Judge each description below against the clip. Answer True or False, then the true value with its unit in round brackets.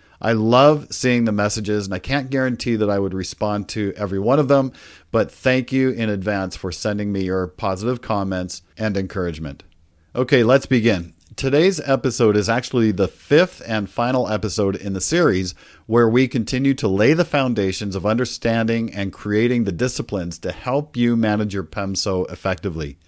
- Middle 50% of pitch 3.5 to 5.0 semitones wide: True (4.5 semitones)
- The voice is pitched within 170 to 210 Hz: False (105 Hz)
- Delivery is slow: False (170 wpm)